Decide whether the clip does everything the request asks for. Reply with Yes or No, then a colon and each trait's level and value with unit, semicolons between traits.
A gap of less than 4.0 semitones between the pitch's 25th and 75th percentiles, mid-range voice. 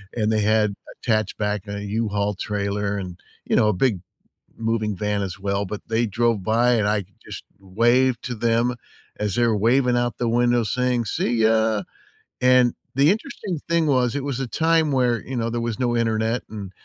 No: average, 2.9 semitones; low, 115 Hz